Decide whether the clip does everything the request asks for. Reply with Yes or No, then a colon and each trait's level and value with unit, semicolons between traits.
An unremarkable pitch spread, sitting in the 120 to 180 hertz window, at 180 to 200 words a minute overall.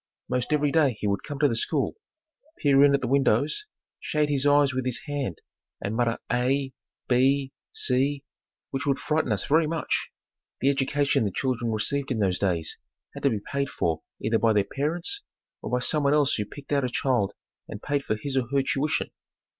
Yes: average, 3.6 semitones; low, 135 Hz; average, 195 wpm